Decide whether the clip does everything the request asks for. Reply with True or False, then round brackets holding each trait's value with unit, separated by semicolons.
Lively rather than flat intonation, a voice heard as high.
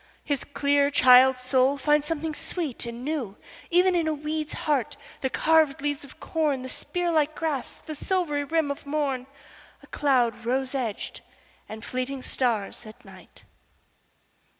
False (3.3 semitones; 280 Hz)